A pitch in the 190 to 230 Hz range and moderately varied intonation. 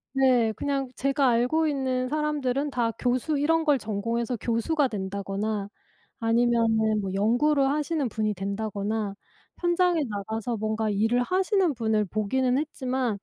No: high, 245 Hz; average, 4.6 semitones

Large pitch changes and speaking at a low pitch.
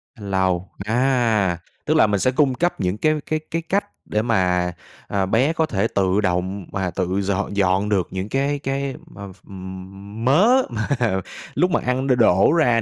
Yes: wide, 6.1 semitones; low, 105 Hz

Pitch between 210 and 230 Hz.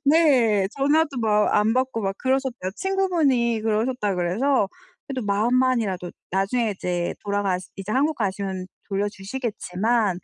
Yes: high, 225 Hz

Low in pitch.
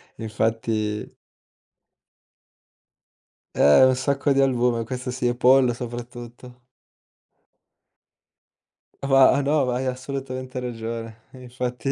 Yes: low, 125 Hz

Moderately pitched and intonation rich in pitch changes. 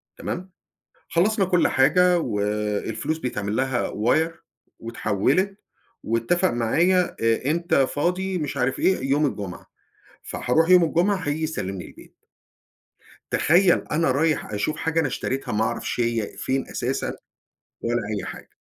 Yes: medium, 145 Hz; wide, 6.8 semitones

